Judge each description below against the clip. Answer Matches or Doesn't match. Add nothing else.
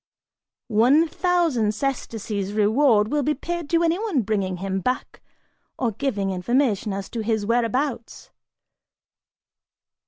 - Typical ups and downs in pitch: Doesn't match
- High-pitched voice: Matches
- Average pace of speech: Doesn't match